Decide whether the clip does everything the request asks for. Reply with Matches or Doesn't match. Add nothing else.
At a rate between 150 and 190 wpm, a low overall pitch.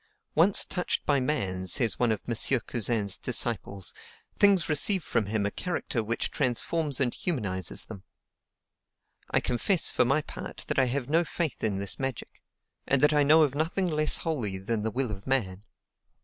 Matches